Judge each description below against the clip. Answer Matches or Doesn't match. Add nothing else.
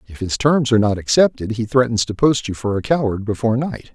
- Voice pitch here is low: Matches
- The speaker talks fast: Matches